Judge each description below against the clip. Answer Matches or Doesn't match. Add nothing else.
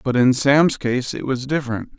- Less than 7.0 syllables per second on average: Matches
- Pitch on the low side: Matches